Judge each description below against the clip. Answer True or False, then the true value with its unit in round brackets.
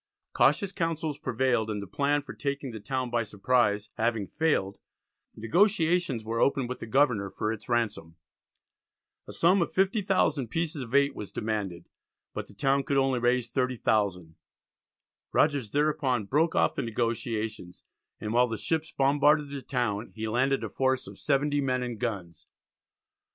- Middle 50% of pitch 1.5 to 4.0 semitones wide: False (4.8 semitones)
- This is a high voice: False (125 Hz)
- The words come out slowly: False (155 wpm)